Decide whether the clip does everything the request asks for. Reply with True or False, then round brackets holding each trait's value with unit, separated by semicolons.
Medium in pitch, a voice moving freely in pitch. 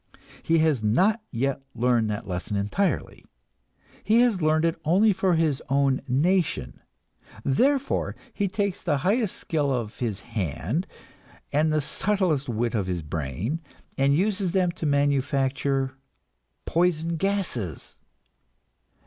True (150 Hz; 7.0 semitones)